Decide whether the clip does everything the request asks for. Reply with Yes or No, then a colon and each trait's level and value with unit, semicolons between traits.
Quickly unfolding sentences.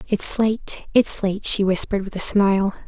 No: average, 190 wpm